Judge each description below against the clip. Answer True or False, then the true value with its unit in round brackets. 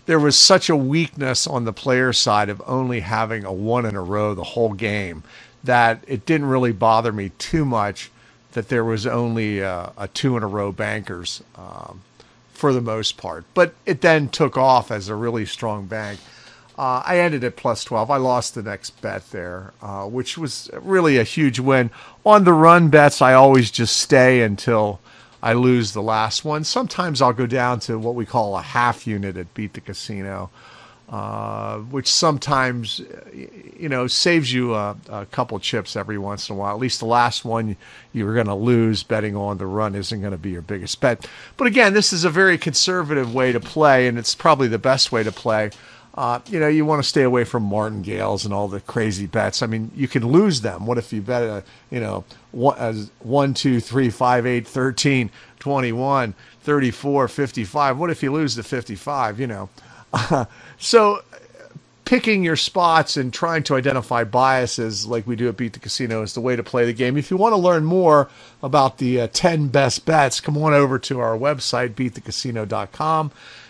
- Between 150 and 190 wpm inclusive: False (200 wpm)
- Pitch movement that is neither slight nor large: True (4.4 semitones)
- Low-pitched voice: True (120 Hz)